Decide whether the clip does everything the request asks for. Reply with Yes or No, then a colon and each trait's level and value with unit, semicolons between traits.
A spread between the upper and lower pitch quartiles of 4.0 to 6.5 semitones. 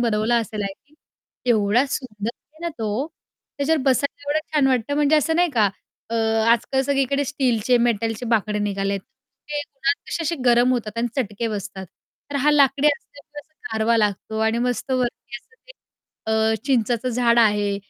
Yes: average, 4.5 semitones